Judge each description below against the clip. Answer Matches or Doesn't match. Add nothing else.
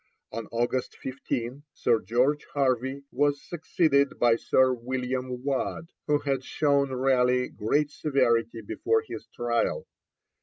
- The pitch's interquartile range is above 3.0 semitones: Doesn't match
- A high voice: Doesn't match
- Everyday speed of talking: Doesn't match